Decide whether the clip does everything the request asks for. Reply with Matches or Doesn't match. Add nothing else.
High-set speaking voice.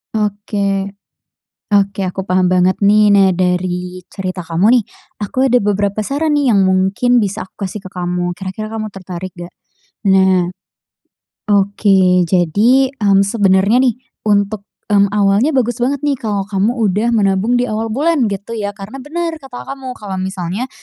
Matches